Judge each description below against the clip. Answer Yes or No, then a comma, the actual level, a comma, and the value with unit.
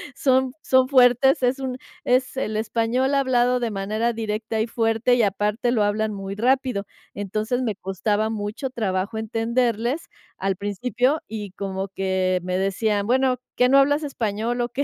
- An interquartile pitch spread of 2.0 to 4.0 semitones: Yes, average, 3.5 semitones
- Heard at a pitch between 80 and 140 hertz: No, high, 225 Hz